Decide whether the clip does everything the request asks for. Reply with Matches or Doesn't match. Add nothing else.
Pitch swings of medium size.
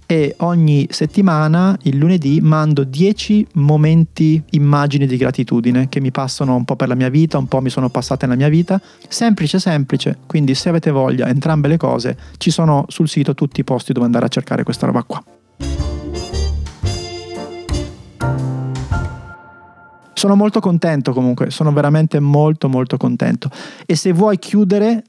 Matches